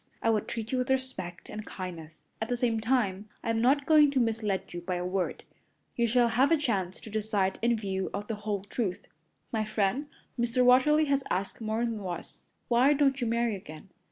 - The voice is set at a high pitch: Yes, high, 225 Hz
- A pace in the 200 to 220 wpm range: Yes, fast, 205 wpm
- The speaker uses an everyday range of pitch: Yes, average, 4.3 semitones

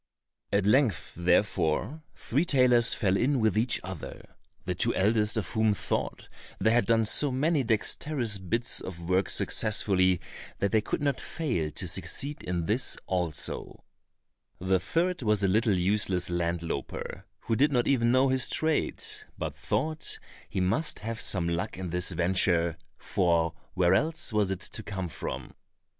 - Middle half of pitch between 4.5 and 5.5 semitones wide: Yes, average, 5.2 semitones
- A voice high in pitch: No, low, 105 Hz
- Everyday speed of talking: Yes, average, 160 wpm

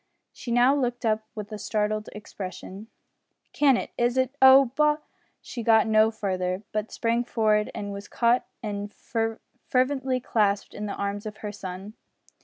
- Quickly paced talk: No, average, 165 wpm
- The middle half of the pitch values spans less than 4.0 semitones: Yes, average, 2.9 semitones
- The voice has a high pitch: Yes, high, 220 Hz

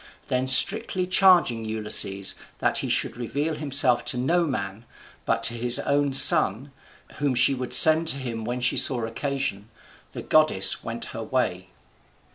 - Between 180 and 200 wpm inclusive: No, average, 155 wpm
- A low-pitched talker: Yes, low, 125 Hz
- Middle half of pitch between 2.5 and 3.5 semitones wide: No, average, 4.2 semitones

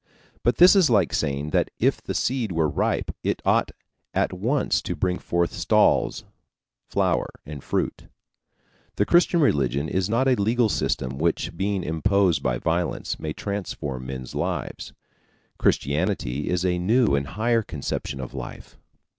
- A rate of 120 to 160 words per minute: Yes, average, 150 wpm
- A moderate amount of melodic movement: No, wide, 7.2 semitones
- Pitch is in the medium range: No, very low, 90 Hz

